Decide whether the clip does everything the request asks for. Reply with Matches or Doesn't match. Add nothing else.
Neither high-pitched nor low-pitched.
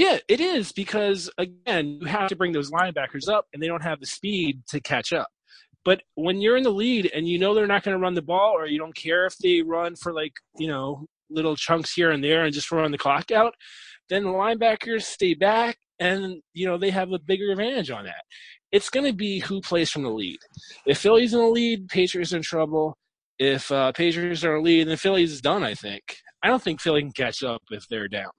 Matches